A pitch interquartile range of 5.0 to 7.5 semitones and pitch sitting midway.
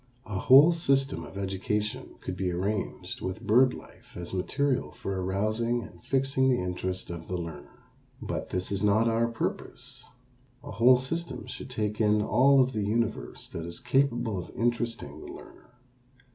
No: average, 5.3 semitones; low, 110 Hz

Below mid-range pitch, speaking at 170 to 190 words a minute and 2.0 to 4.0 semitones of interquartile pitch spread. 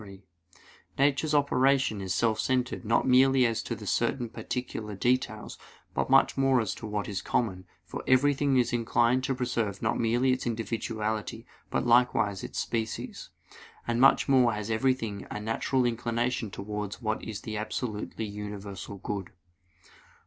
No: low, 115 Hz; average, 150 wpm; average, 3.4 semitones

